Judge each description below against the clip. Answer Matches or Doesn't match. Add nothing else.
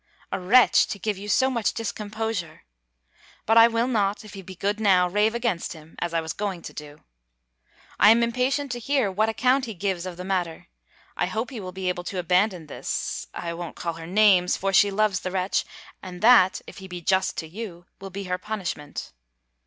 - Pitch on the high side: Matches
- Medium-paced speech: Doesn't match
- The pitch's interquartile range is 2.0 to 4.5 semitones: Matches